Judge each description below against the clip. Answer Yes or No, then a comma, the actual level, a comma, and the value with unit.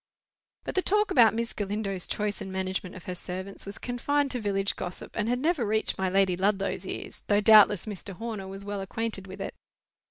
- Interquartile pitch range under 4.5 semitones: Yes, average, 2.9 semitones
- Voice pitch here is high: Yes, high, 205 Hz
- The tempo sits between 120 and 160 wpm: No, average, 200 wpm